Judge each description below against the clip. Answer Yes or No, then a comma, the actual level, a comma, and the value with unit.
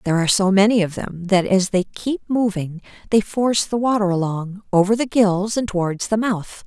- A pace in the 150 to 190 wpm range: No, fast, 205 wpm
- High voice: Yes, high, 200 Hz